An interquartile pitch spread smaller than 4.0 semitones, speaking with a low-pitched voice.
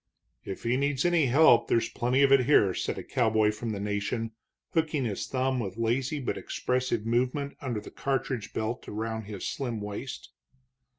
Yes: average, 3.6 semitones; low, 120 Hz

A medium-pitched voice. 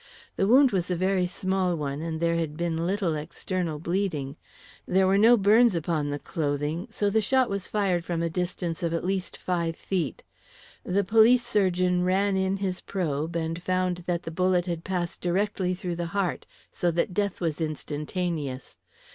Yes: medium, 180 Hz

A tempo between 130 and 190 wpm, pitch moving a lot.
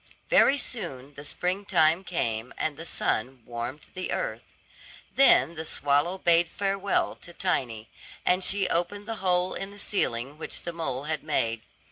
Yes: average, 160 wpm; wide, 5.8 semitones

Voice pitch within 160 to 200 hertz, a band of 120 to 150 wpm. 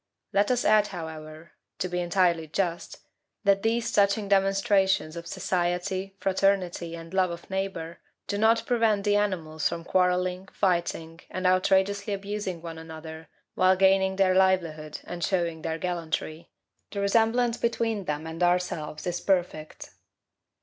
Yes: medium, 185 Hz; average, 140 wpm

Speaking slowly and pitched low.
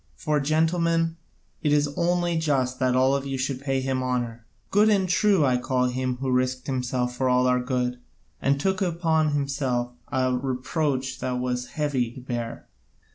No: average, 170 wpm; low, 130 Hz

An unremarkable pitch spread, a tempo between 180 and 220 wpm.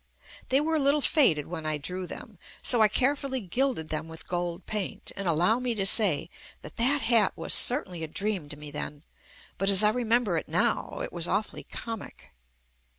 No: wide, 6.8 semitones; average, 200 wpm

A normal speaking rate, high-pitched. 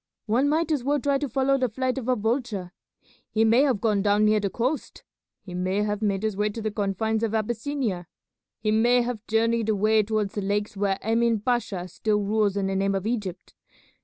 No: fast, 210 wpm; high, 215 Hz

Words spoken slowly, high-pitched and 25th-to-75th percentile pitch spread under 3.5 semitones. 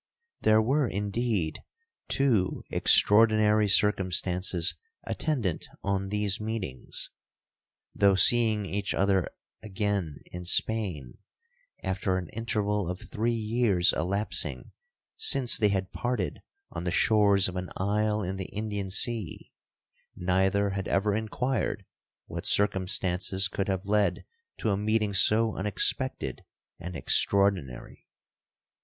No: slow, 110 wpm; low, 100 Hz; narrow, 2.5 semitones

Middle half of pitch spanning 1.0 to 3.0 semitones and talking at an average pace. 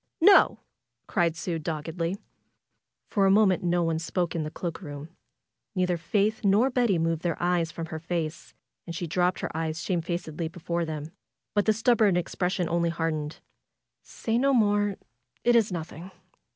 No: average, 3.4 semitones; average, 160 wpm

